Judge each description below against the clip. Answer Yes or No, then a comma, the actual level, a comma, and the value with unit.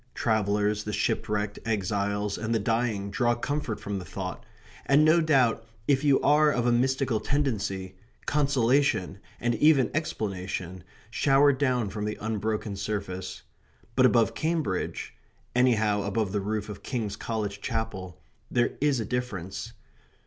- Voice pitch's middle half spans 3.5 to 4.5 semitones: Yes, average, 4.2 semitones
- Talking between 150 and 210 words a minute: No, average, 140 wpm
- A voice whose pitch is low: Yes, low, 110 Hz